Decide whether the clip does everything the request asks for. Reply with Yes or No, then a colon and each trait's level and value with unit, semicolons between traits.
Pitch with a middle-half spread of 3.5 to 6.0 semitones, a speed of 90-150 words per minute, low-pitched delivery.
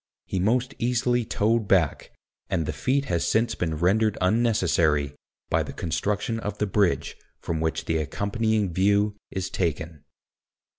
Yes: average, 4.9 semitones; average, 145 wpm; low, 100 Hz